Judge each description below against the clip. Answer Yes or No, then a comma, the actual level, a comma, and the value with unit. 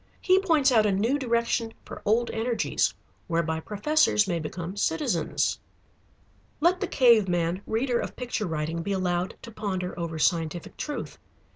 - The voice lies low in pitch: No, high, 205 Hz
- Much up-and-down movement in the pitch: Yes, wide, 5.9 semitones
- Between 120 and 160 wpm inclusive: Yes, average, 150 wpm